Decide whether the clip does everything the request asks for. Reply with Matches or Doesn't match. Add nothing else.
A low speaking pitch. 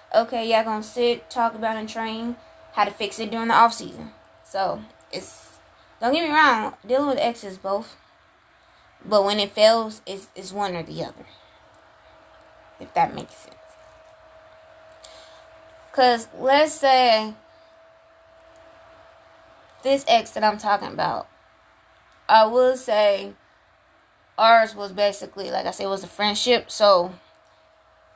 Doesn't match